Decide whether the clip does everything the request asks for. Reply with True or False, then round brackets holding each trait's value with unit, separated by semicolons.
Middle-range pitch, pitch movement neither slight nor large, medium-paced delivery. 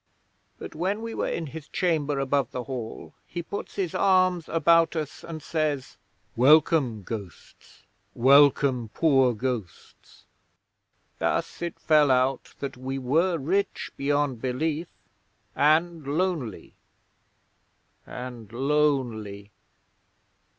False (145 Hz; 4.4 semitones; 110 wpm)